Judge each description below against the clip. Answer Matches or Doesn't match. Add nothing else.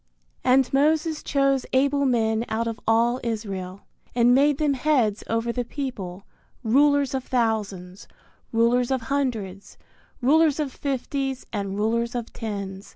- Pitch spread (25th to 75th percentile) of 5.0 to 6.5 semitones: Doesn't match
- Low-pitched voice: Doesn't match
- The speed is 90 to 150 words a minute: Matches